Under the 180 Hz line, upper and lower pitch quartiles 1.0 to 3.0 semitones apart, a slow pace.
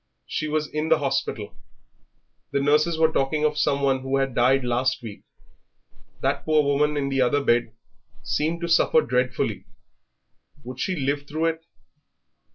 No: medium, 140 Hz; narrow, 2.5 semitones; average, 160 wpm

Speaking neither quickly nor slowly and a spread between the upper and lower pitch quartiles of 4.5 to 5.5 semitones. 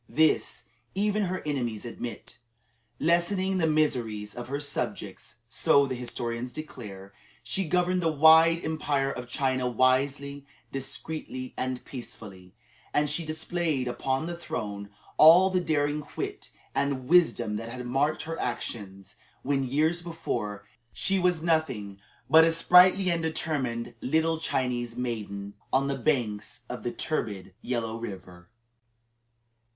No: slow, 130 wpm; average, 5.2 semitones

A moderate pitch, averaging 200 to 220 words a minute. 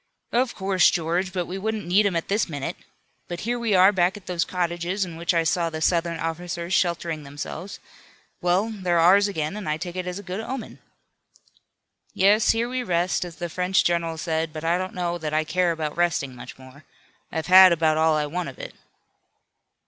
Yes: medium, 175 Hz; fast, 205 wpm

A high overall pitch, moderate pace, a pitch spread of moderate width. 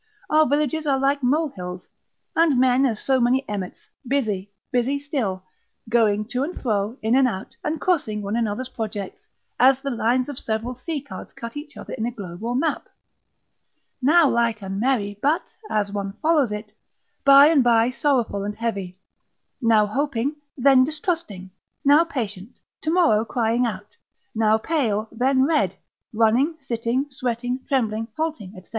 Yes: high, 245 Hz; average, 155 wpm; average, 4.7 semitones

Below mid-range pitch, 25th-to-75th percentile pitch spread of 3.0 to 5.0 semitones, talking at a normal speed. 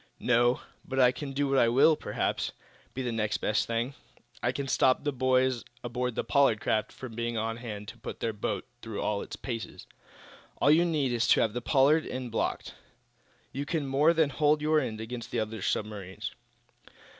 Yes: low, 125 Hz; average, 3.5 semitones; average, 190 wpm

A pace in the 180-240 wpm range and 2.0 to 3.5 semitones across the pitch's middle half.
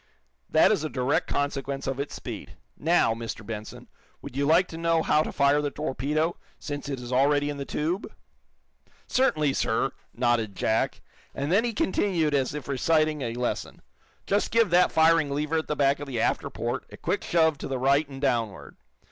Yes: average, 190 wpm; average, 3.1 semitones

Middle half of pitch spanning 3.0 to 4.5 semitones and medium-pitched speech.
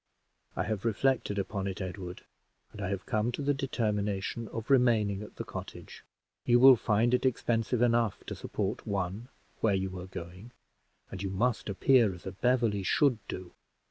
No: average, 3.8 semitones; low, 105 Hz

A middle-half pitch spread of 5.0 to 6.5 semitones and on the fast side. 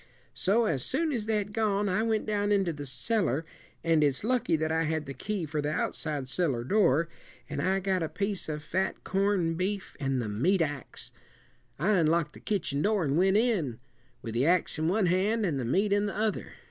Yes: wide, 5.4 semitones; fast, 210 wpm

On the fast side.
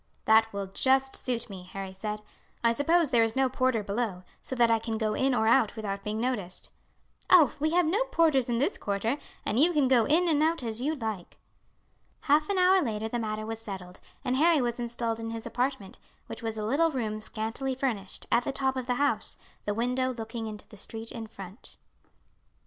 Yes: fast, 210 wpm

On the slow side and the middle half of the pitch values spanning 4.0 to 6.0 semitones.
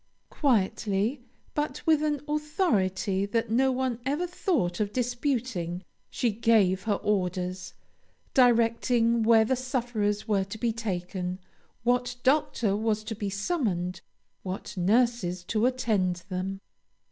Yes: slow, 125 wpm; average, 4.6 semitones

